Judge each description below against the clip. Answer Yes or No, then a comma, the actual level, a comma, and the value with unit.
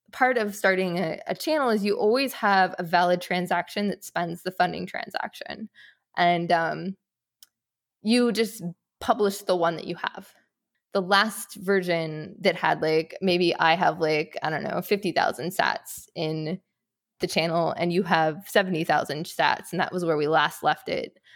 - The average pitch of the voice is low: No, medium, 185 Hz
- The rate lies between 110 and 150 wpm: No, average, 165 wpm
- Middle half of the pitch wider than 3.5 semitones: No, average, 3.2 semitones